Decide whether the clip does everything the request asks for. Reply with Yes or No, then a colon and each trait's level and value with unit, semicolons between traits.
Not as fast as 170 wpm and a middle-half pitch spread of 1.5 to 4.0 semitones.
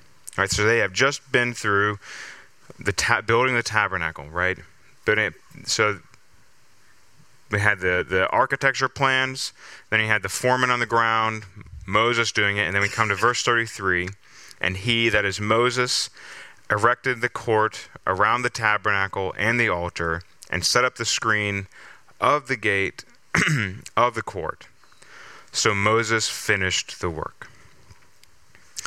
Yes: average, 150 wpm; average, 3.4 semitones